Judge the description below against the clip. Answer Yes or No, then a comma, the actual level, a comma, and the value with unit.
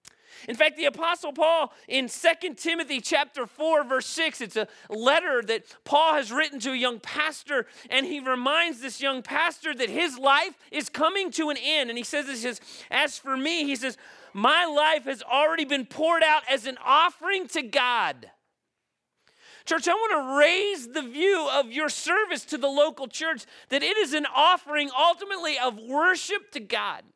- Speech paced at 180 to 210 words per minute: Yes, average, 185 wpm